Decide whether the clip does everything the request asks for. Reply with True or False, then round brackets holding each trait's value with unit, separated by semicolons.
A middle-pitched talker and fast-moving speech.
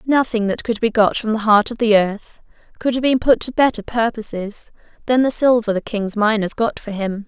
False (225 Hz; 225 wpm)